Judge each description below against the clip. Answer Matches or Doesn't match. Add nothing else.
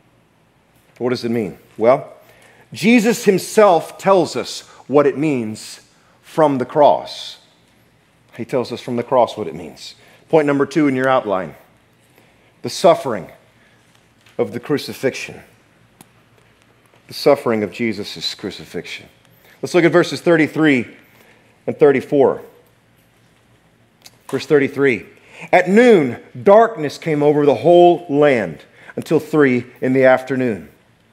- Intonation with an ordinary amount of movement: Matches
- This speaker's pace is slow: Matches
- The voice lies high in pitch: Doesn't match